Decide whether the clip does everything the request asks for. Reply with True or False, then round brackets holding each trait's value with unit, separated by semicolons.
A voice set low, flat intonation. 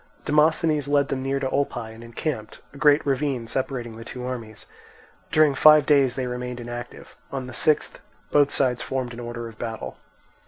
False (130 Hz; 3.2 semitones)